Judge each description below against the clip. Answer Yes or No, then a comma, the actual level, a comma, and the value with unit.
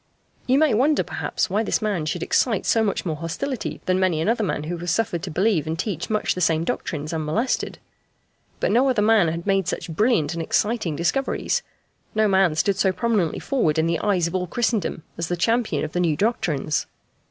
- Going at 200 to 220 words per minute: Yes, fast, 205 wpm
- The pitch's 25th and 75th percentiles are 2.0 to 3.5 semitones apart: No, average, 5.2 semitones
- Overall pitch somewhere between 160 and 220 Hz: Yes, medium, 185 Hz